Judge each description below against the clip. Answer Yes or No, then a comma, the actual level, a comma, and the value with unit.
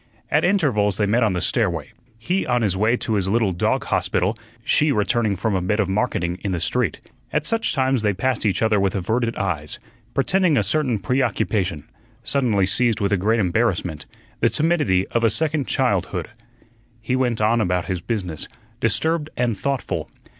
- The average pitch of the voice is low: Yes, low, 110 Hz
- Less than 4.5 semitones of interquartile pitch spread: No, average, 4.9 semitones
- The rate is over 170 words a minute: Yes, average, 180 wpm